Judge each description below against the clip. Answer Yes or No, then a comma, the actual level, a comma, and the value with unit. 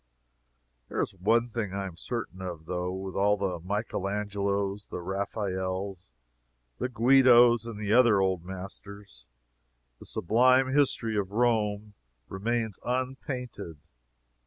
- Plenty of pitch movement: No, average, 3.7 semitones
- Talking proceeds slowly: Yes, slow, 125 wpm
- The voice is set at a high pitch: No, low, 100 Hz